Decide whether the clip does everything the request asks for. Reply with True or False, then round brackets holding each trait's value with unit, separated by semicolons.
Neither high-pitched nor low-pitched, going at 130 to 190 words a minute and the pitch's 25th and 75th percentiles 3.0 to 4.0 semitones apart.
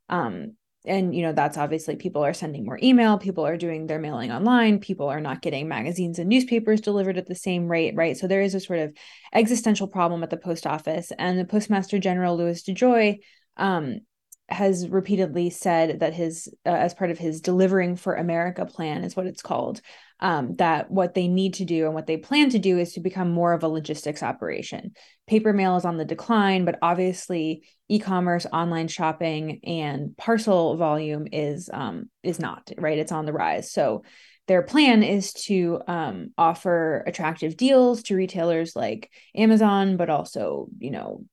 True (180 Hz; 185 wpm; 3.3 semitones)